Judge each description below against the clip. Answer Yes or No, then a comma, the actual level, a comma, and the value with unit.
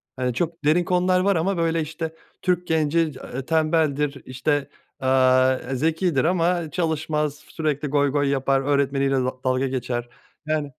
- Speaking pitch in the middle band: Yes, medium, 150 Hz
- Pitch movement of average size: Yes, average, 3.4 semitones